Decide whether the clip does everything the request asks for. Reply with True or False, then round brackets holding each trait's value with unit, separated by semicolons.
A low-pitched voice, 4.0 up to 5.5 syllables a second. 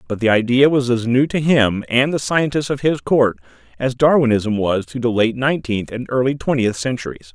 True (125 Hz; 5.2 syllables/s)